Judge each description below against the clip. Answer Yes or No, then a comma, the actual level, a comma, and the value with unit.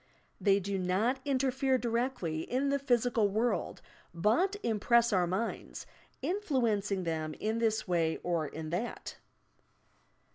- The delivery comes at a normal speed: No, slow, 130 wpm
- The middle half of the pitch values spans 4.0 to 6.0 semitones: Yes, wide, 5.6 semitones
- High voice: Yes, high, 220 Hz